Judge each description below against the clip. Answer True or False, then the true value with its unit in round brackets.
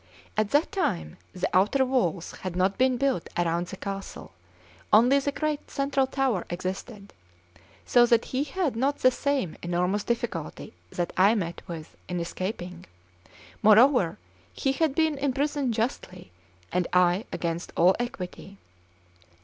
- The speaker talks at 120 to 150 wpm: True (140 wpm)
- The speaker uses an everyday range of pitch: False (7.0 semitones)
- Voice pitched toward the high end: True (215 Hz)